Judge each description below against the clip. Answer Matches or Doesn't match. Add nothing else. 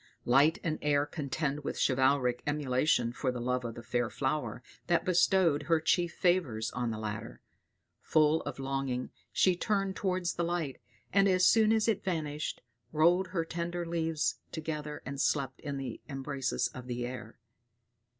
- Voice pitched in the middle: Matches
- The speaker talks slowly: Doesn't match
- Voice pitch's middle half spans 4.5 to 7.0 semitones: Matches